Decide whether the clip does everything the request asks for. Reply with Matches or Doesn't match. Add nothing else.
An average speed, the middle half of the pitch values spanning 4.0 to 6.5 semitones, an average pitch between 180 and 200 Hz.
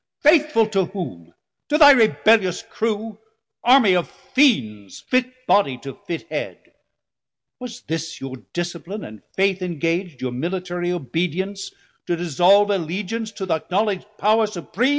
Doesn't match